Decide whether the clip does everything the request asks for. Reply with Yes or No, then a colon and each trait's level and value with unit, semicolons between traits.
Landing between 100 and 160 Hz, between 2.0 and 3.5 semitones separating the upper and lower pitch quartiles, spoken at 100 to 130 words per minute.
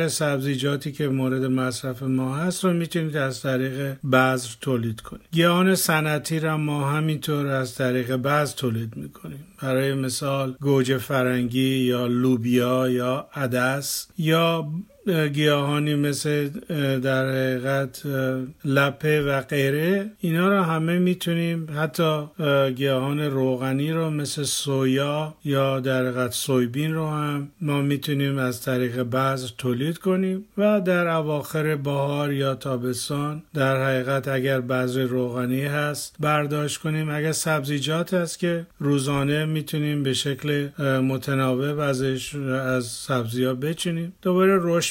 Yes: medium, 140 Hz; average, 2.8 semitones; average, 120 wpm